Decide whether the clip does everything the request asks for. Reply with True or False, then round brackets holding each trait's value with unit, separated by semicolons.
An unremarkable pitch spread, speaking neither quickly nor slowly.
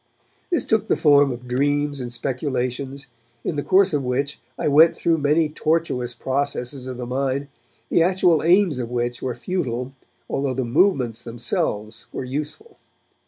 True (3.8 semitones; 160 wpm)